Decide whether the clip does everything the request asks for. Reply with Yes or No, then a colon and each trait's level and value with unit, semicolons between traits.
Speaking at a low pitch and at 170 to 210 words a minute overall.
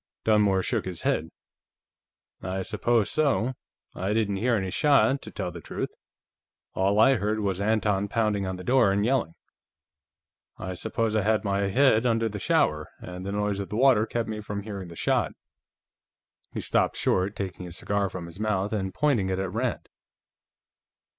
Yes: low, 105 Hz; average, 175 wpm